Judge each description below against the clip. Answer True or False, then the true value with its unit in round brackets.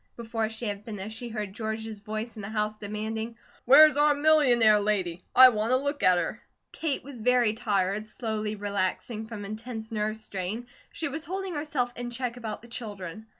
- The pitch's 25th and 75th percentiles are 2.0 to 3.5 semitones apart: True (2.7 semitones)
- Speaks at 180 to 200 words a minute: True (185 wpm)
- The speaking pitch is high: True (220 Hz)